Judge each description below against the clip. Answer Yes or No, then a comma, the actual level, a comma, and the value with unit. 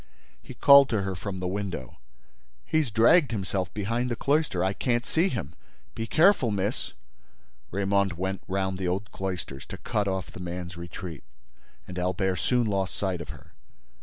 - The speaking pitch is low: Yes, very low, 95 Hz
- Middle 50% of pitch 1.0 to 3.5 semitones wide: No, average, 3.9 semitones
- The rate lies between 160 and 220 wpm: Yes, average, 165 wpm